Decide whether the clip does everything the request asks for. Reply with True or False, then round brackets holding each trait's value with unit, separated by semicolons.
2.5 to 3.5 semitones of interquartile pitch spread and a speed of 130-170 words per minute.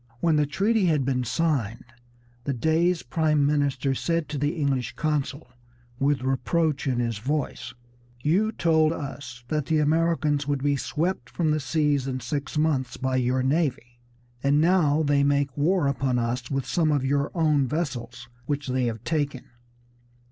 True (3.2 semitones; 160 wpm)